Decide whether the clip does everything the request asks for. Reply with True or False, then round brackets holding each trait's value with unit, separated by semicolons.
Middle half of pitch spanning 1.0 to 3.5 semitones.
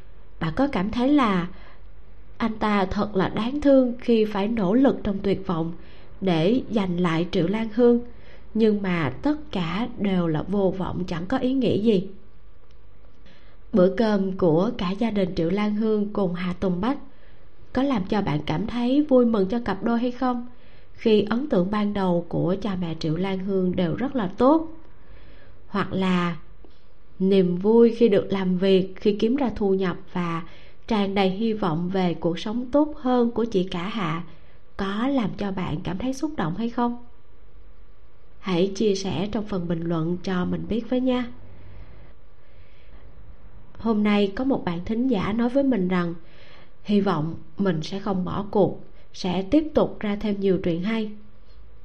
False (4.7 semitones)